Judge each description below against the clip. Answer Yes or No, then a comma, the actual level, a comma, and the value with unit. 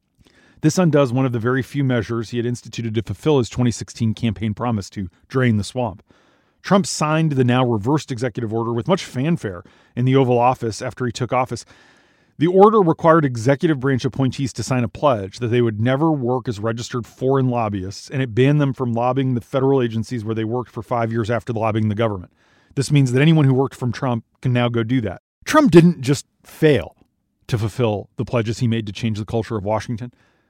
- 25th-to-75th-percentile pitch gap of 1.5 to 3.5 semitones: Yes, average, 2.8 semitones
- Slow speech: No, fast, 205 wpm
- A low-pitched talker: Yes, low, 125 Hz